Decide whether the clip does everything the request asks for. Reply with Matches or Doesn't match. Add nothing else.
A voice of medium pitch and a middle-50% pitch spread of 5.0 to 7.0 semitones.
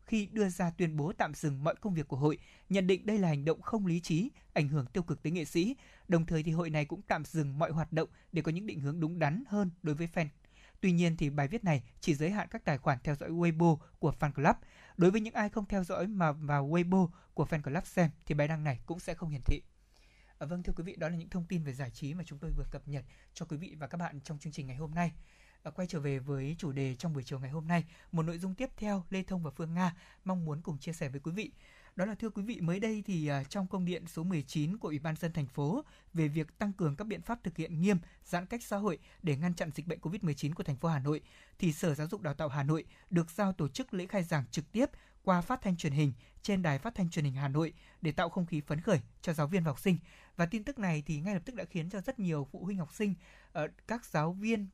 Doesn't match